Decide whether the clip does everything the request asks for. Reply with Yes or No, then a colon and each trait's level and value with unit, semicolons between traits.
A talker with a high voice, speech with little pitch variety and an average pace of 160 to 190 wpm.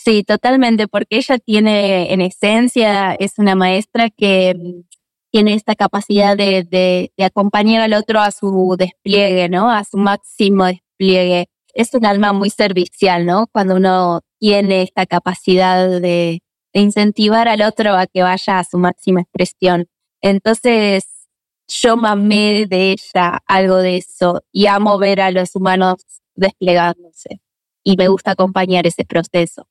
No: high, 195 Hz; narrow, 2.2 semitones; average, 145 wpm